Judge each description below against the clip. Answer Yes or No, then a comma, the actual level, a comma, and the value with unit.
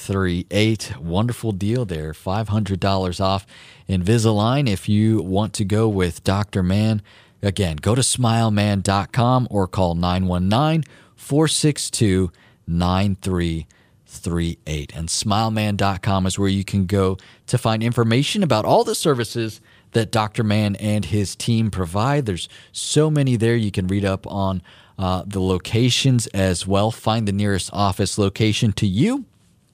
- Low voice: Yes, low, 105 Hz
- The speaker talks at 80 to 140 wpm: Yes, slow, 135 wpm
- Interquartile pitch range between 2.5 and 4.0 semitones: Yes, average, 3.2 semitones